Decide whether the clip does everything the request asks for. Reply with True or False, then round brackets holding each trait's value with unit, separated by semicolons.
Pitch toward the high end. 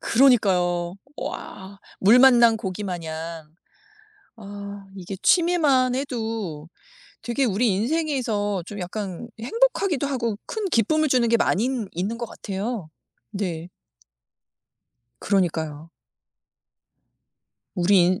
True (205 Hz)